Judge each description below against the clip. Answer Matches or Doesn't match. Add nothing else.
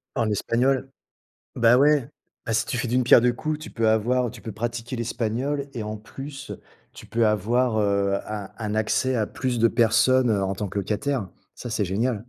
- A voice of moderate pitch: Doesn't match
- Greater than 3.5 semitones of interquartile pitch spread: Doesn't match